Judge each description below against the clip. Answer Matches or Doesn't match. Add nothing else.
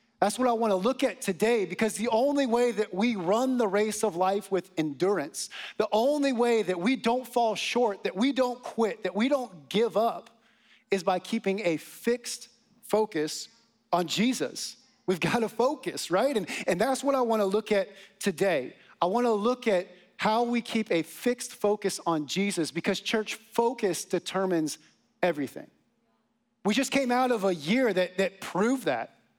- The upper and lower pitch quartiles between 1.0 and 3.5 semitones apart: Doesn't match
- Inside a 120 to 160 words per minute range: Doesn't match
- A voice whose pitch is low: Doesn't match